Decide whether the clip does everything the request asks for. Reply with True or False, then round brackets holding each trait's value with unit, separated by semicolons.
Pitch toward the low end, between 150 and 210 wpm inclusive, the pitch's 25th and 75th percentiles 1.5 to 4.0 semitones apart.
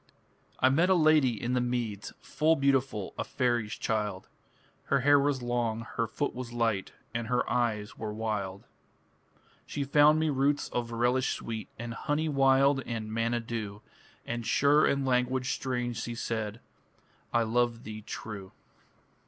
True (120 Hz; 155 wpm; 3.3 semitones)